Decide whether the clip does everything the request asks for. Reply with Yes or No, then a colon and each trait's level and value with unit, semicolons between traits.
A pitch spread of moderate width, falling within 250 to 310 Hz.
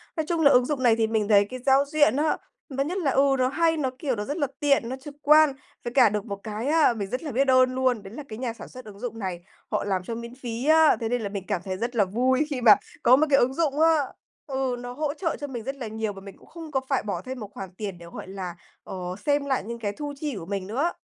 Yes: average, 5.0 semitones; very high, 255 Hz